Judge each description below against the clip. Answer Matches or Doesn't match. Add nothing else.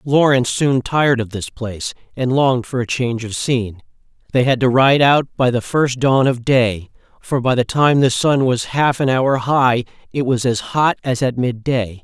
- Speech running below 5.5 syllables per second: Matches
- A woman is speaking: Doesn't match